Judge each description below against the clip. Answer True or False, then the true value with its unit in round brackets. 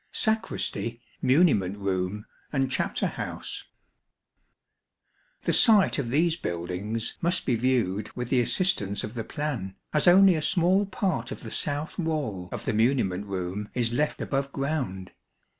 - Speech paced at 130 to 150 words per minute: True (140 wpm)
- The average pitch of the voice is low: True (130 Hz)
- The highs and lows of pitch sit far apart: True (7.5 semitones)